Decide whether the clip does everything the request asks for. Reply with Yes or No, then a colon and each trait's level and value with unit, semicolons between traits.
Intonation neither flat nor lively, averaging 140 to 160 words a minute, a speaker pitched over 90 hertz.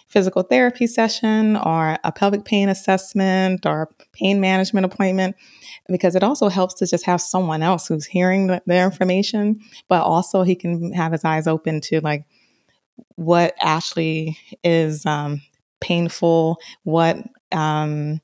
Yes: average, 3.4 semitones; average, 145 wpm; medium, 185 Hz